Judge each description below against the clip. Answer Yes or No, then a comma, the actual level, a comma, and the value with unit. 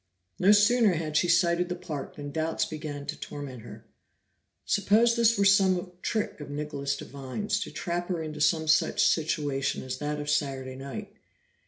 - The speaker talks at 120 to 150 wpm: No, average, 170 wpm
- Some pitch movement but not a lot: Yes, average, 4.7 semitones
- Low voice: No, medium, 155 Hz